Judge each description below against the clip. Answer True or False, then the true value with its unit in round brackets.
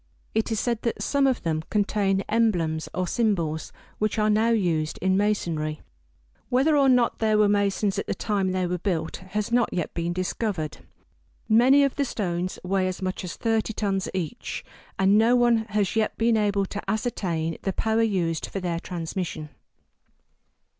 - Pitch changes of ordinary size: True (3.8 semitones)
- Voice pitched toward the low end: False (200 Hz)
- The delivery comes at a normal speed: True (175 wpm)